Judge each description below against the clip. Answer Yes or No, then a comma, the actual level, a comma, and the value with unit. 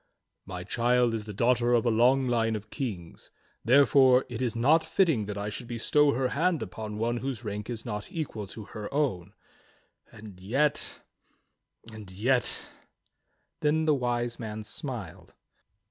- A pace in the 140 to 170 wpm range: Yes, average, 165 wpm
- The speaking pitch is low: Yes, low, 120 Hz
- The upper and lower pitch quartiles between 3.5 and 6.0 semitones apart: Yes, average, 3.8 semitones